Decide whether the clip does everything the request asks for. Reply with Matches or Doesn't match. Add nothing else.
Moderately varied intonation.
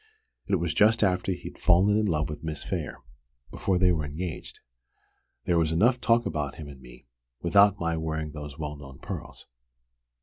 Matches